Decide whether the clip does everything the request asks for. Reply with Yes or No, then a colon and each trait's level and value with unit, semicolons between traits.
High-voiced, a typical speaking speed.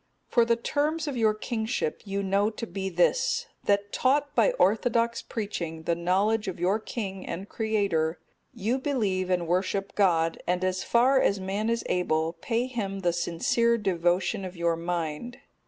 Yes: high, 200 Hz; average, 165 wpm